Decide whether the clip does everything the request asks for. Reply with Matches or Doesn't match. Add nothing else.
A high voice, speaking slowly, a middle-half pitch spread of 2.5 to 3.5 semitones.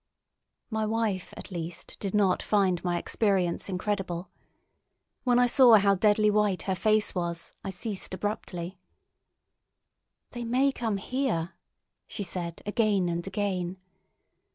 Matches